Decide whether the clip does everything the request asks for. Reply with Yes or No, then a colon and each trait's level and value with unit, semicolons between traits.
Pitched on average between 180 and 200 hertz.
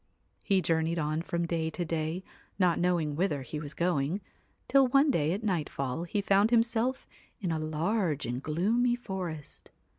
No: medium, 170 Hz